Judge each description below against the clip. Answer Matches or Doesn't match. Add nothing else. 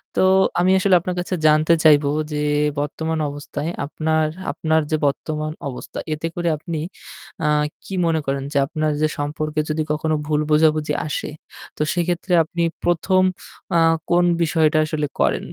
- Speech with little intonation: Matches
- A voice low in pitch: Doesn't match